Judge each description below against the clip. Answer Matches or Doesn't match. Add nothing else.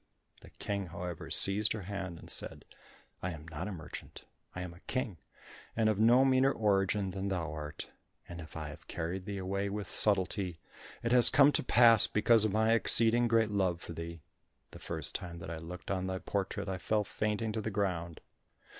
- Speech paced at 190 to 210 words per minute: Matches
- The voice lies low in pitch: Matches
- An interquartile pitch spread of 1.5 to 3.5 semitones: Doesn't match